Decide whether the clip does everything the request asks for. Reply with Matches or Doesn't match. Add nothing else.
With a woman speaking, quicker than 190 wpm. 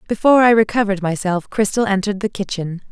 Doesn't match